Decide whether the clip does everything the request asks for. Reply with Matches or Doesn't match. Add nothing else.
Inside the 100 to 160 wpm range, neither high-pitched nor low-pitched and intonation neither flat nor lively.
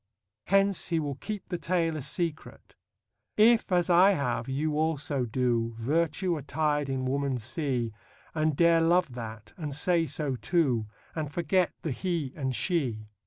Matches